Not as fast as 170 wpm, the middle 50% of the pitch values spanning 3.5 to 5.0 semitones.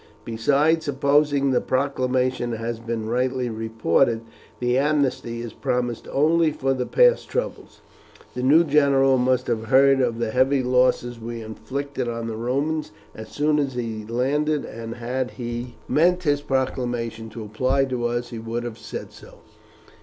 No: average, 155 wpm; average, 3.0 semitones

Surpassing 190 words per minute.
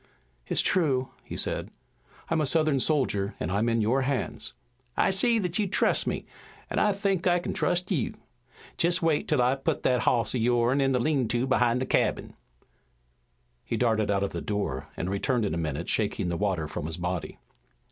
Yes: average, 200 wpm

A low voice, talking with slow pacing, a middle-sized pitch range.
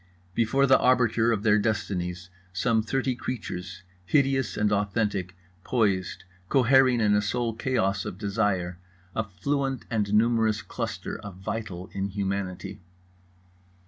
Yes: low, 105 Hz; slow, 120 wpm; average, 3.7 semitones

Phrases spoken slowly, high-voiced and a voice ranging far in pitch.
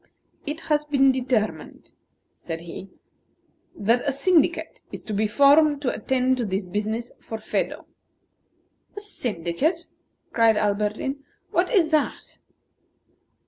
Yes: slow, 120 wpm; very high, 250 Hz; wide, 5.9 semitones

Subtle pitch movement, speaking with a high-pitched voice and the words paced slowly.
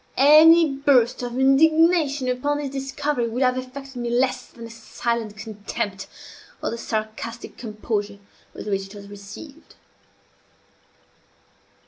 No: average, 4.1 semitones; very high, 250 Hz; slow, 125 wpm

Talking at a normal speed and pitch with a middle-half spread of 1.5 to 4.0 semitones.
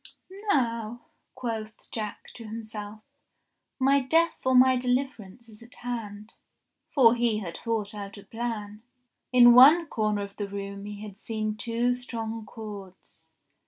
Yes: average, 145 wpm; average, 2.8 semitones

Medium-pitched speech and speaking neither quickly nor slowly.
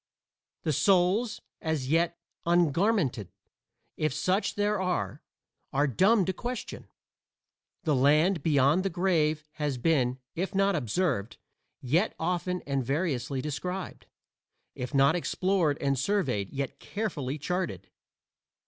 No: medium, 160 Hz; slow, 115 wpm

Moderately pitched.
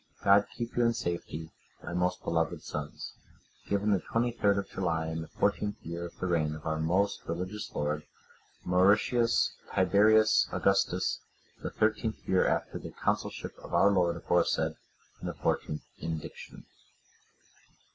No: very low, 90 Hz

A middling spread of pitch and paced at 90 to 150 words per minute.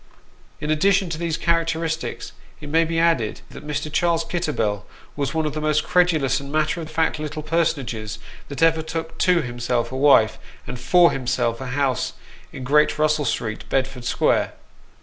No: average, 3.8 semitones; average, 170 wpm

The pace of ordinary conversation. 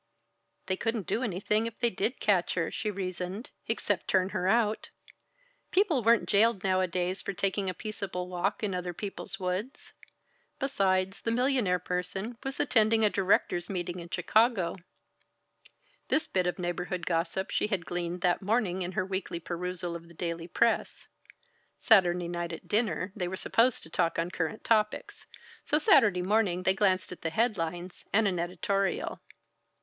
Yes: average, 160 wpm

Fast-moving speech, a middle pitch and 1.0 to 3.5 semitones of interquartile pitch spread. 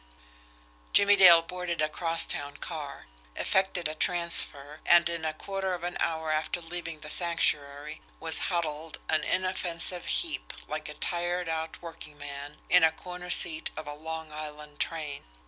No: average, 155 wpm; medium, 165 Hz; narrow, 2.4 semitones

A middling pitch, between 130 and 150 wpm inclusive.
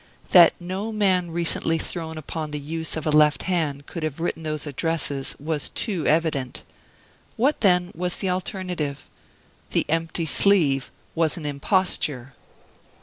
Yes: medium, 165 Hz; average, 145 wpm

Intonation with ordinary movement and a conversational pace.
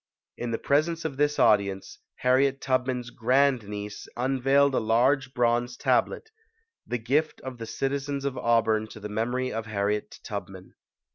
Yes: average, 3.5 semitones; average, 155 wpm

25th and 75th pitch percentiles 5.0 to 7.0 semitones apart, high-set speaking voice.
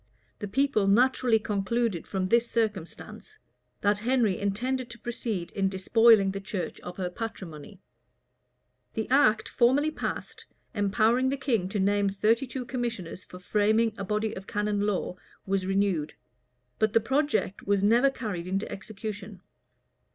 No: average, 3.4 semitones; high, 210 Hz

